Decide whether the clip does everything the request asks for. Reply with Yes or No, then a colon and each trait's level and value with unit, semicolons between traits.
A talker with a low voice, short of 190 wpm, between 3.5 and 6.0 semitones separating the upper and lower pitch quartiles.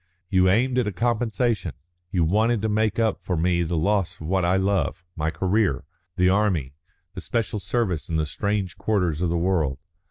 No: very low, 95 Hz; average, 195 wpm; average, 4.1 semitones